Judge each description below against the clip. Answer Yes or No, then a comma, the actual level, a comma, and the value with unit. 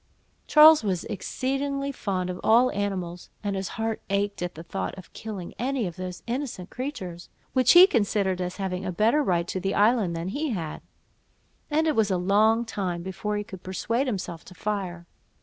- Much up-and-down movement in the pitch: No, average, 4.6 semitones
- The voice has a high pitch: Yes, high, 200 Hz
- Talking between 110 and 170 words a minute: No, average, 185 wpm